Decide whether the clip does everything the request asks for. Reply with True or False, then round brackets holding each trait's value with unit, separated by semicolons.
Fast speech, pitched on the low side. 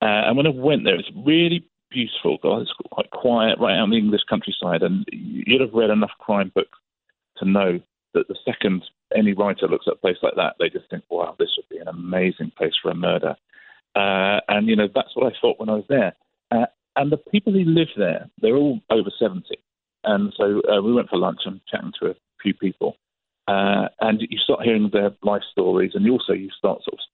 True (230 wpm; 110 Hz)